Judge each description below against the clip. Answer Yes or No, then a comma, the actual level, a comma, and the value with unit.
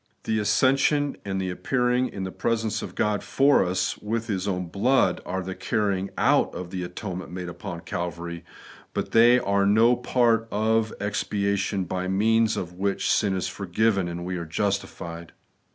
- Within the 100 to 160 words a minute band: No, average, 175 wpm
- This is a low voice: Yes, low, 100 Hz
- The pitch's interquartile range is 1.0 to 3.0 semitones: No, average, 3.6 semitones